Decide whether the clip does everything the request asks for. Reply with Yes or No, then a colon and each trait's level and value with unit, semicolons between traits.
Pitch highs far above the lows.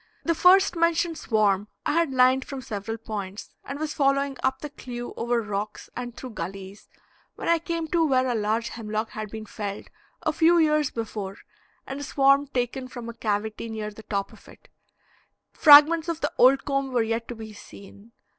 No: average, 4.9 semitones